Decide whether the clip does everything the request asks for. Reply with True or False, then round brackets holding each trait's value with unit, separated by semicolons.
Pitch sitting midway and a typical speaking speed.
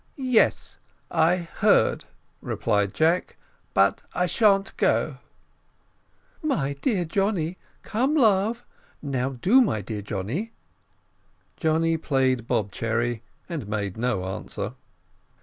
False (160 Hz; 105 wpm)